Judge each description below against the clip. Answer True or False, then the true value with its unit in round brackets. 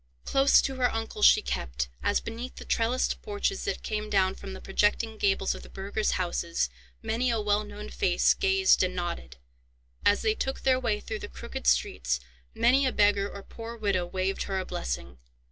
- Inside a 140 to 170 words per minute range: False (190 wpm)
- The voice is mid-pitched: False (205 Hz)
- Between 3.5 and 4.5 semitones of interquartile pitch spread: True (4.2 semitones)